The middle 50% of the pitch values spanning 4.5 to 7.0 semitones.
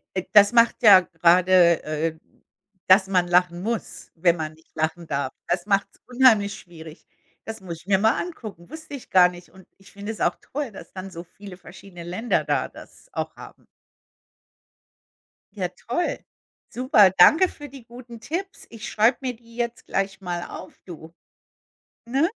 Yes: average, 5.1 semitones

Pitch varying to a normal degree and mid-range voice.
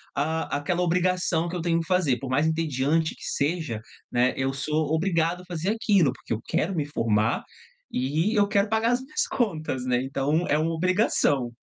Yes: average, 4.7 semitones; medium, 160 Hz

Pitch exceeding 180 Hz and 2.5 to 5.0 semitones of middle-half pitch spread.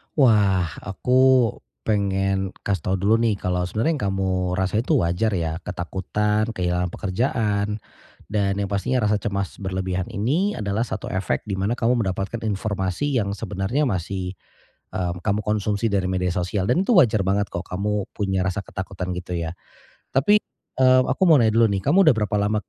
No: low, 100 Hz; average, 3.2 semitones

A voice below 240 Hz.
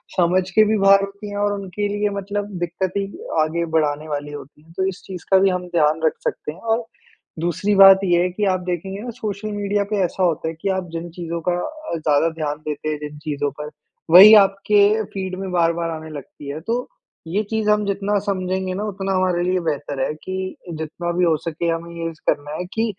Yes: medium, 185 Hz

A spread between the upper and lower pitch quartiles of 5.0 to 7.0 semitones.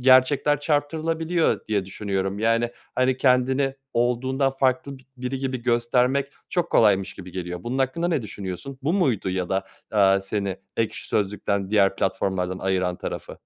Yes: wide, 5.6 semitones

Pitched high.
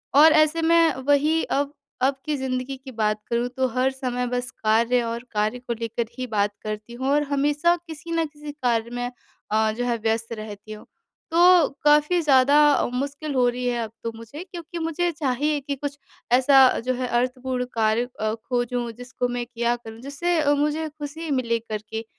Yes: very high, 255 Hz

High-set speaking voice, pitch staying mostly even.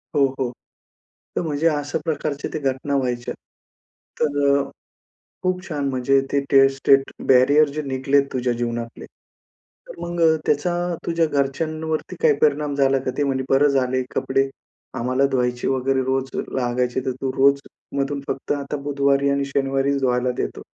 No: medium, 140 Hz; narrow, 1.7 semitones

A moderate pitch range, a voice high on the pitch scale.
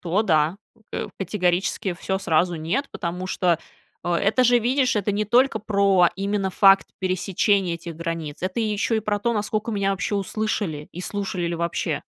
Yes: average, 3.3 semitones; high, 195 Hz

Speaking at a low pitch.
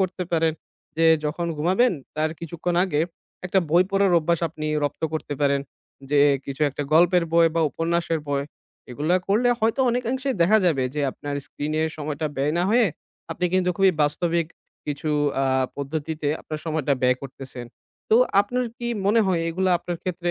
No: medium, 165 Hz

